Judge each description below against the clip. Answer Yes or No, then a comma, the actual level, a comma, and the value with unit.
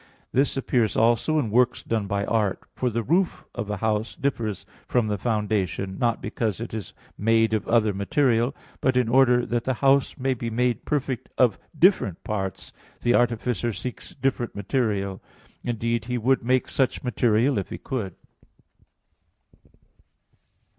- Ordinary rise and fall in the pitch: Yes, average, 3.1 semitones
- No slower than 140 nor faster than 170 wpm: Yes, average, 155 wpm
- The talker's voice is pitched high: No, low, 115 Hz